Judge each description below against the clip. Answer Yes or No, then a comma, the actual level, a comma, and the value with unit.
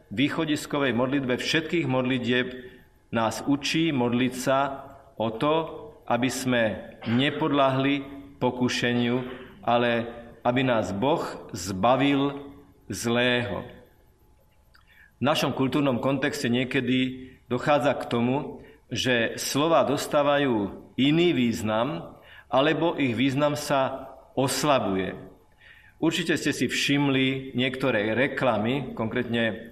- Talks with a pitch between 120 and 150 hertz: Yes, low, 130 Hz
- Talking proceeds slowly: Yes, slow, 90 wpm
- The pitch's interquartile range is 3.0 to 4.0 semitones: No, narrow, 2.4 semitones